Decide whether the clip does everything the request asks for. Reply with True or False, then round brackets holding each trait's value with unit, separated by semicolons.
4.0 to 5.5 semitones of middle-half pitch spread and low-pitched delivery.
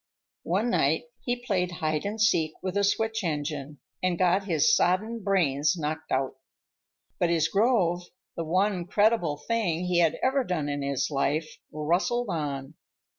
False (4.8 semitones; 175 Hz)